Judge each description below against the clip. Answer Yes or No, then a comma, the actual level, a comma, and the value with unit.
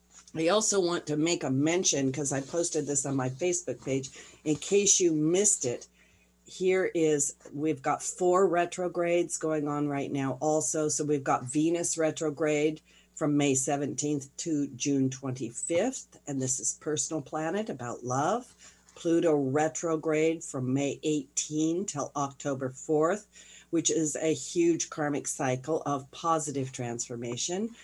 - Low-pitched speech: No, medium, 155 Hz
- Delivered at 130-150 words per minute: Yes, average, 140 wpm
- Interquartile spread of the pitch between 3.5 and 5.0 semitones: No, average, 3.1 semitones